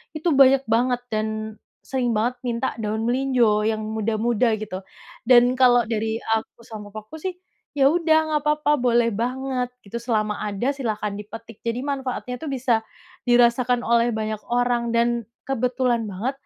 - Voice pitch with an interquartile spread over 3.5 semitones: No, narrow, 2.6 semitones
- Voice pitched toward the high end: Yes, high, 240 Hz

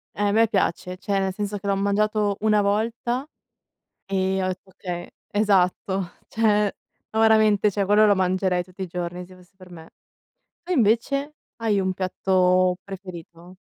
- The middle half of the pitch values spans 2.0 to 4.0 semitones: Yes, narrow, 2.4 semitones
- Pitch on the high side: Yes, high, 195 Hz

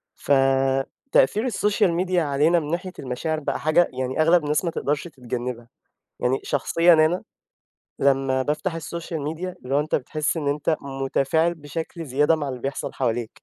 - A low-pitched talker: No, medium, 150 Hz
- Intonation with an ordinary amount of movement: Yes, average, 3.7 semitones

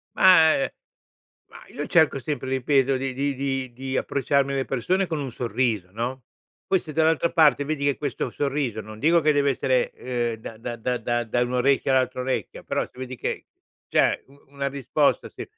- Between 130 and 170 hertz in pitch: Yes, low, 135 Hz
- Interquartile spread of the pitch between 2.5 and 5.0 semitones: Yes, average, 2.8 semitones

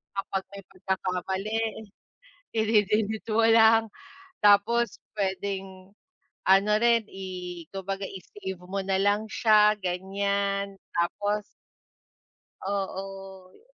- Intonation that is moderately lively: No, narrow, 1.8 semitones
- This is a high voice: Yes, high, 195 Hz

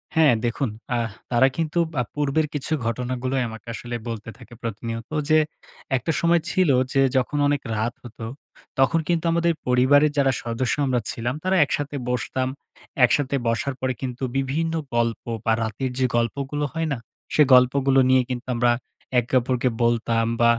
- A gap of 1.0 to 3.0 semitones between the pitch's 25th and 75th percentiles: No, average, 3.4 semitones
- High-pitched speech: No, low, 130 Hz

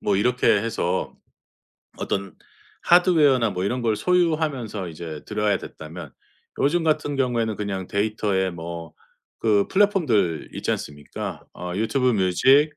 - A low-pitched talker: Yes, low, 105 Hz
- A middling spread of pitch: No, wide, 6.6 semitones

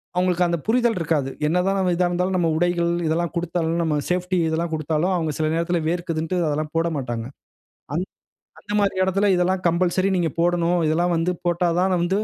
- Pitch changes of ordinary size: No, narrow, 1.8 semitones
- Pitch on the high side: No, medium, 175 Hz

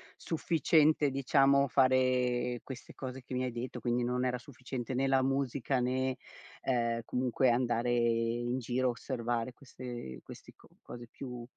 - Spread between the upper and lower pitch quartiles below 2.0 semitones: Yes, narrow, 1.6 semitones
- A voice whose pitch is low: Yes, low, 125 Hz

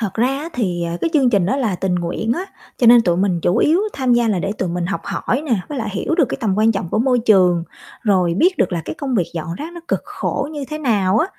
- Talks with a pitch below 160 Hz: No, high, 220 Hz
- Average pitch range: No, wide, 6.6 semitones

